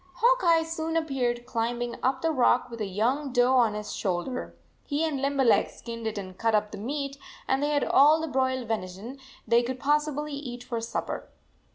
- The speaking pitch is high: Yes, very high, 255 Hz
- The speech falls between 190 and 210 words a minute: Yes, average, 200 wpm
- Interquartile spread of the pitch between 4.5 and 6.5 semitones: No, average, 4.0 semitones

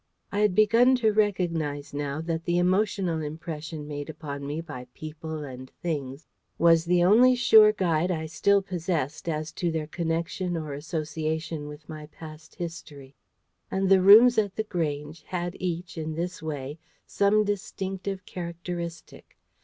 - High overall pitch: No, medium, 165 Hz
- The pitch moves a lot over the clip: No, average, 3.4 semitones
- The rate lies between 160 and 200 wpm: No, average, 150 wpm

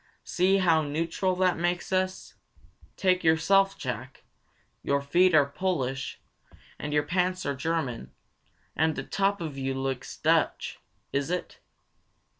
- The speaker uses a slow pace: Yes, slow, 130 wpm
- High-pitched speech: No, medium, 165 Hz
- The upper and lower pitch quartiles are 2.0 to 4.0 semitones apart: No, average, 4.7 semitones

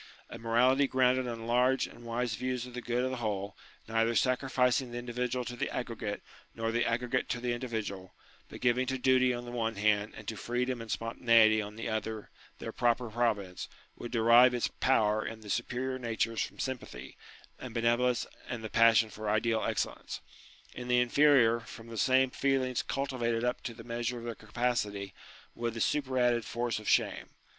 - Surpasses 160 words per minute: Yes, average, 185 wpm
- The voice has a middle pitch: No, low, 120 Hz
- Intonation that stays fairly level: Yes, narrow, 1.8 semitones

